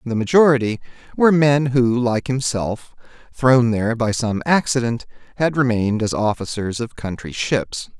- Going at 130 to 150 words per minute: Yes, average, 145 wpm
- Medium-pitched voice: No, low, 120 Hz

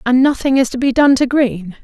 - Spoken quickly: Yes, fast, 260 wpm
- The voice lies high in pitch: Yes, very high, 255 Hz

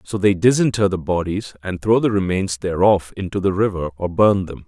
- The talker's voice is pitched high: No, very low, 95 Hz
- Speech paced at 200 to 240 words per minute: Yes, fast, 205 wpm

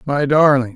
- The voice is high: No, medium, 140 Hz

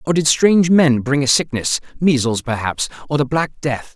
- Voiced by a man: Yes, male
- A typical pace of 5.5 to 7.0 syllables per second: No, 5.0 syllables/s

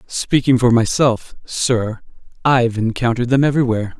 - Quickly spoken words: No, slow, 120 wpm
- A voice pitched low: Yes, low, 120 Hz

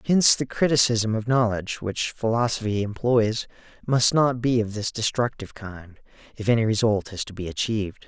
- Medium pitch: No, low, 110 Hz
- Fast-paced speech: No, average, 165 wpm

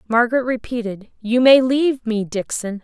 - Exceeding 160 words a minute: No, average, 150 wpm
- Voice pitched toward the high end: Yes, high, 235 Hz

